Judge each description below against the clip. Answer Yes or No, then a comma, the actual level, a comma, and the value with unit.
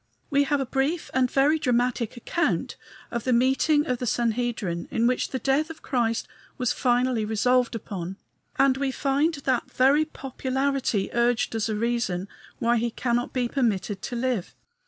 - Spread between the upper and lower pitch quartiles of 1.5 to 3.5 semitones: Yes, narrow, 2.6 semitones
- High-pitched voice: Yes, very high, 250 Hz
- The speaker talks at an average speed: Yes, average, 165 wpm